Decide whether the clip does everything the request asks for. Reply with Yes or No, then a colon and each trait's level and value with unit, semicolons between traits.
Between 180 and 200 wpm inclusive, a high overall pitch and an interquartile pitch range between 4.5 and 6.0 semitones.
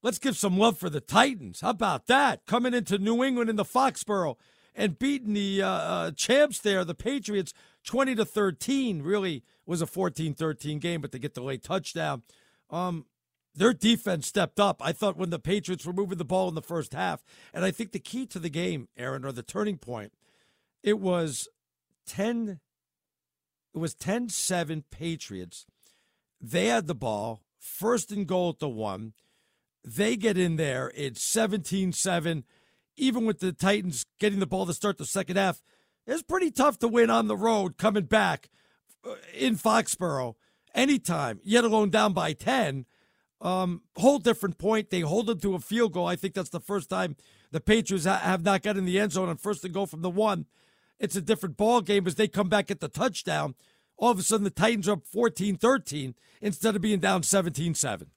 Yes: average, 190 wpm; high, 195 Hz; average, 4.8 semitones